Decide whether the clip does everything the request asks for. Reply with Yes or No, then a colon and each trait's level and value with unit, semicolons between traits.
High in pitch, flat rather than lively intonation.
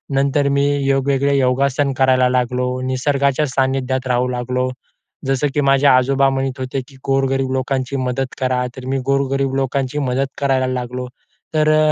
No: low, 135 Hz; narrow, 1.3 semitones